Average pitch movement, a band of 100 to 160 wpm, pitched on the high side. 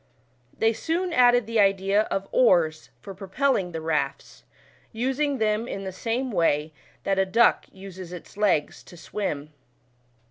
Yes: average, 4.8 semitones; average, 150 wpm; high, 195 Hz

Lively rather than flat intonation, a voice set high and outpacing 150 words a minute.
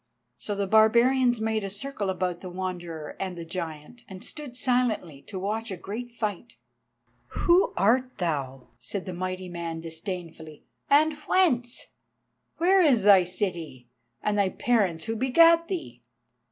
No: wide, 5.8 semitones; high, 200 Hz; average, 145 wpm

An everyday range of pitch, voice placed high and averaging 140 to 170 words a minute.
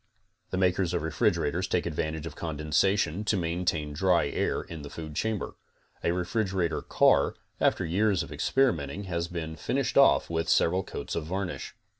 No: average, 3.0 semitones; very low, 85 Hz; average, 160 wpm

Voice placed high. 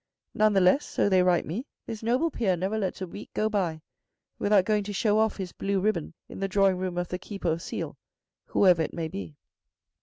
Yes: high, 195 Hz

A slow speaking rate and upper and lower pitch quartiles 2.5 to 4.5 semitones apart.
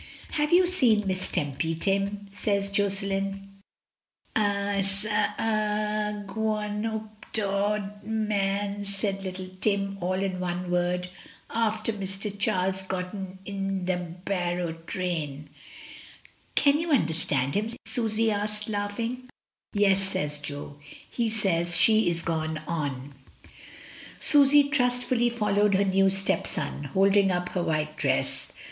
Yes: slow, 125 wpm; average, 2.8 semitones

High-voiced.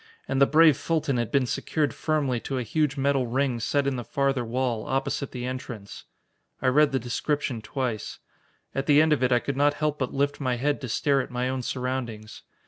No: low, 130 Hz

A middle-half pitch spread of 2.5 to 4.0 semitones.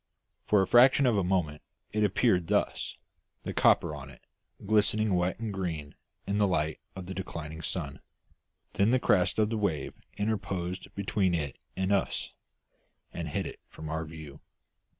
No: average, 4.4 semitones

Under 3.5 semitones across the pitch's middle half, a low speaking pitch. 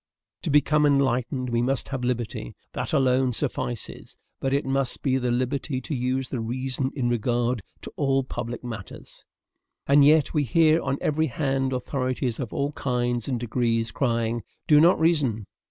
Yes: narrow, 2.5 semitones; low, 130 Hz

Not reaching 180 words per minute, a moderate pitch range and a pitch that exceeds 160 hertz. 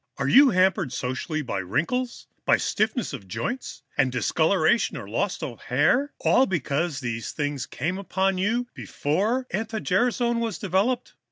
No: average, 150 wpm; wide, 8.5 semitones; high, 190 Hz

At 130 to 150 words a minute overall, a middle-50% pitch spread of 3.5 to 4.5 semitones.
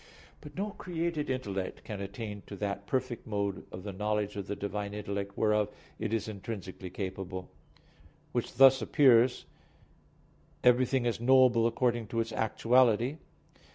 Yes: average, 140 wpm; average, 3.9 semitones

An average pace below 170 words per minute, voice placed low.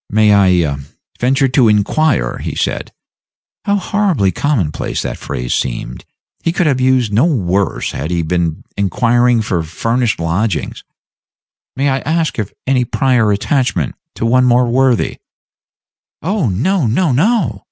Yes: average, 140 wpm; low, 120 Hz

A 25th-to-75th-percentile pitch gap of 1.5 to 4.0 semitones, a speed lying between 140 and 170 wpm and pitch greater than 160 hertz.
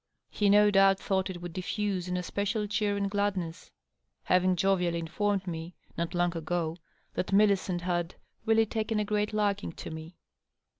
Yes: average, 2.8 semitones; average, 165 wpm; high, 190 Hz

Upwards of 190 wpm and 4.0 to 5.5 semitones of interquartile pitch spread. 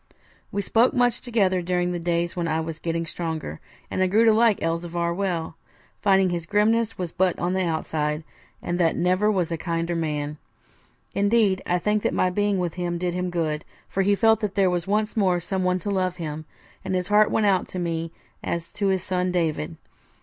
No: fast, 205 wpm; average, 3.0 semitones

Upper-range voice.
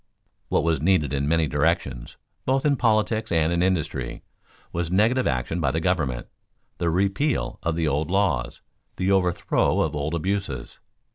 No: very low, 85 Hz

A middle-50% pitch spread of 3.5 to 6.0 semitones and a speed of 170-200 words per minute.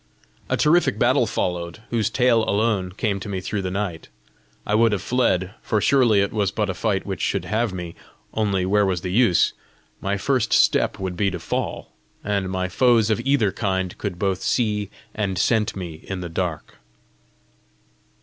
No: average, 3.0 semitones; average, 180 wpm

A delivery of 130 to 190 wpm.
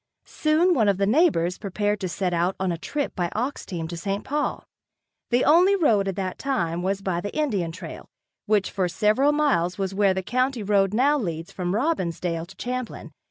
No: average, 200 wpm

